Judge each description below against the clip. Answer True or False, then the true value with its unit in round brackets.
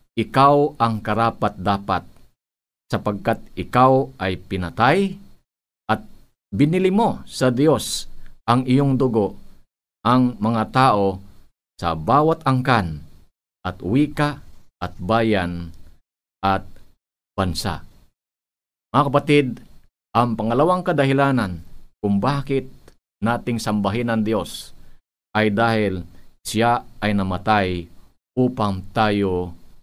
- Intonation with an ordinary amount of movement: False (5.7 semitones)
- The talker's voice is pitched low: True (110 Hz)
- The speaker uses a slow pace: True (90 wpm)